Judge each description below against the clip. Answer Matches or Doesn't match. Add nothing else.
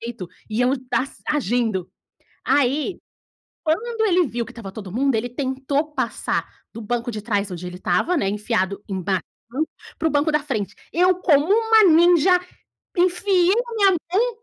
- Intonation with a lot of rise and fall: Matches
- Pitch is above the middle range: Matches